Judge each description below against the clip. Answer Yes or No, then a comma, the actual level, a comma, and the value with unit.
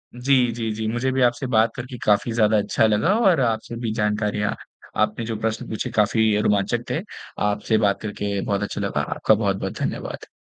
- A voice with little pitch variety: Yes, narrow, 2.3 semitones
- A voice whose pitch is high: No, low, 110 Hz